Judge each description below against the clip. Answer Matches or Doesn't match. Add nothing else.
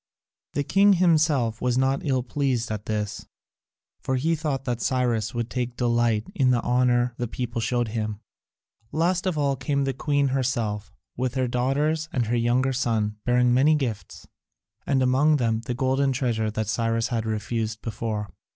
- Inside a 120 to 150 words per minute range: Doesn't match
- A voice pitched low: Matches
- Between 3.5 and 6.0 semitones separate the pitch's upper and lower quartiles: Doesn't match